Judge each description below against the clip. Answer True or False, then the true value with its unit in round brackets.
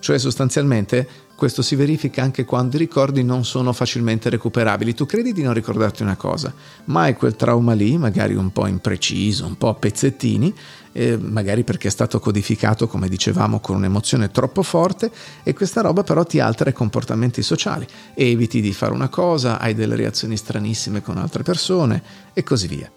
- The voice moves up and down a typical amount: True (3.8 semitones)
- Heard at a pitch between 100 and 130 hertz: True (120 Hz)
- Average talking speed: False (185 wpm)